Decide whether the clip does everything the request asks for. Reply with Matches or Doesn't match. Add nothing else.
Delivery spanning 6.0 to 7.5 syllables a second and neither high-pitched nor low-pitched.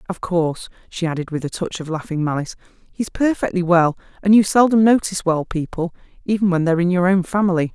Matches